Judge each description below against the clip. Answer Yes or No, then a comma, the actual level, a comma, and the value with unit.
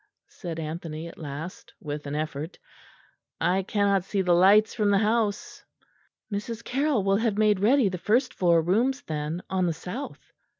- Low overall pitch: No, high, 190 Hz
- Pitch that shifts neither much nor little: Yes, average, 4.5 semitones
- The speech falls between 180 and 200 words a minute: No, average, 165 wpm